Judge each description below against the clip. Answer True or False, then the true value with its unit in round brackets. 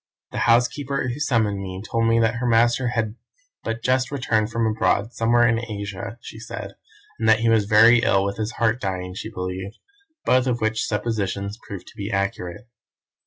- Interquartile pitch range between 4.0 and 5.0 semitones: False (2.7 semitones)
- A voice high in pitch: False (110 Hz)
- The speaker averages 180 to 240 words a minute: True (185 wpm)